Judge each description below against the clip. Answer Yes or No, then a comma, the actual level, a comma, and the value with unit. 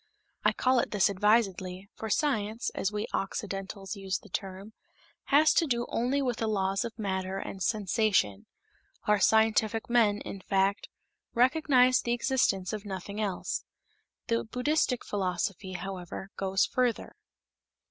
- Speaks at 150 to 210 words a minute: No, slow, 135 wpm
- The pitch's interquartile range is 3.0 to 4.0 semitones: Yes, average, 3.6 semitones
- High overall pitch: Yes, high, 210 Hz